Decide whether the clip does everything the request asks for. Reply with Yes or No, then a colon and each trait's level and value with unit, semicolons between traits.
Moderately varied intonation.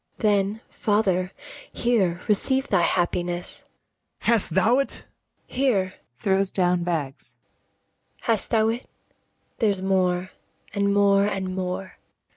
Yes: average, 3.0 semitones